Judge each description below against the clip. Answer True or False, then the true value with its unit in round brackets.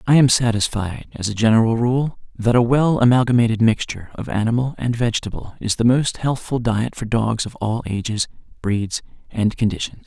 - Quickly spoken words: False (175 wpm)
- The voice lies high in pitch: False (115 Hz)